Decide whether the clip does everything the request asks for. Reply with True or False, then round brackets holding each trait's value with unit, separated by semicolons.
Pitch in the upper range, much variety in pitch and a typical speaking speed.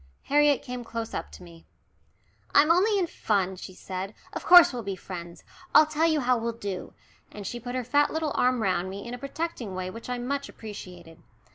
False (235 Hz; 7.1 semitones; 210 wpm)